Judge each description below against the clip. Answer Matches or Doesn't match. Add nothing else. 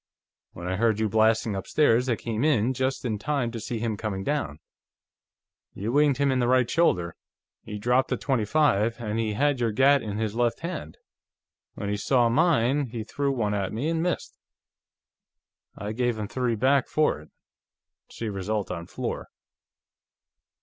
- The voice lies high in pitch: Doesn't match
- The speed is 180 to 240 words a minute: Doesn't match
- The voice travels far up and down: Doesn't match